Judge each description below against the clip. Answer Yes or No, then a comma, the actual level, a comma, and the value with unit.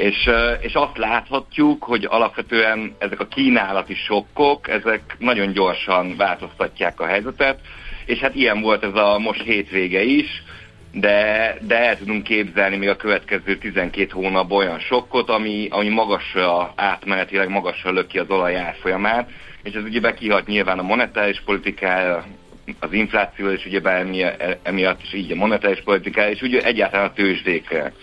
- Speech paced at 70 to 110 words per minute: No, average, 150 wpm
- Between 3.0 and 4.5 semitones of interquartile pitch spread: No, narrow, 2.5 semitones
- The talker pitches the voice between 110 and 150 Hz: No, low, 100 Hz